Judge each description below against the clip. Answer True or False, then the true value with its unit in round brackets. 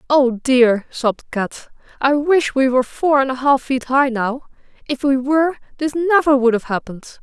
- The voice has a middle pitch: False (270 Hz)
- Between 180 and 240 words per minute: True (190 wpm)